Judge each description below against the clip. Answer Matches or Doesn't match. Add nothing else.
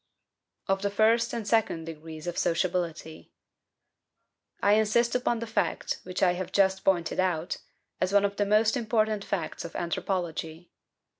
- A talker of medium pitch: Doesn't match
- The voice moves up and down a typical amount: Matches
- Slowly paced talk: Doesn't match